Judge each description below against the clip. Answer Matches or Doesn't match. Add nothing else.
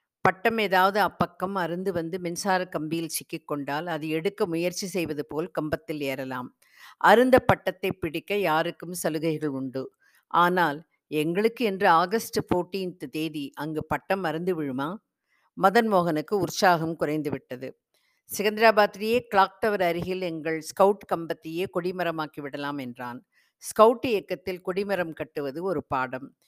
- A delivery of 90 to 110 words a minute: Doesn't match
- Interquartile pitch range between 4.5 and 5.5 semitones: Doesn't match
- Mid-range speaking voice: Matches